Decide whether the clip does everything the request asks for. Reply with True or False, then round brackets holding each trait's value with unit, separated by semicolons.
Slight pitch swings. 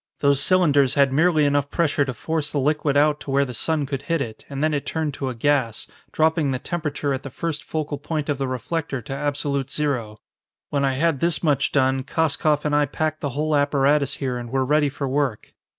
True (2.0 semitones)